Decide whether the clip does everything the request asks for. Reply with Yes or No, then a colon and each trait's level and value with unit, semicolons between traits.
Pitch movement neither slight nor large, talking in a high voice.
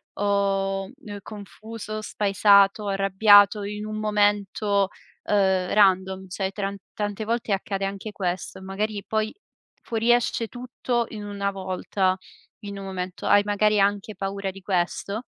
No: narrow, 1.5 semitones; high, 200 Hz